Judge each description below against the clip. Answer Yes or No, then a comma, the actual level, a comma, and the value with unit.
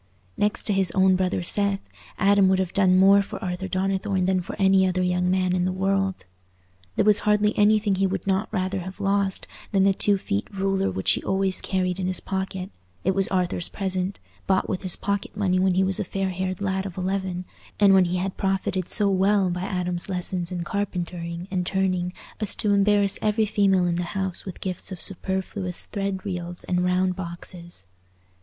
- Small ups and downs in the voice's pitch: Yes, narrow, 1.3 semitones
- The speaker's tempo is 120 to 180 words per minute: No, average, 200 wpm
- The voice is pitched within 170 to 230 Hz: Yes, high, 190 Hz